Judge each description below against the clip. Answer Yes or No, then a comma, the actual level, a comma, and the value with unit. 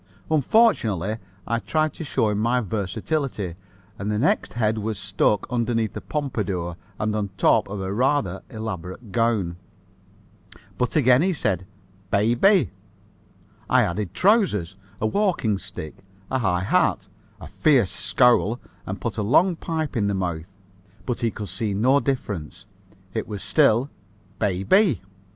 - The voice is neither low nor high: No, low, 110 Hz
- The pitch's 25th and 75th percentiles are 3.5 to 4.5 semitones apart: No, average, 5.1 semitones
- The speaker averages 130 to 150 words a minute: Yes, average, 145 wpm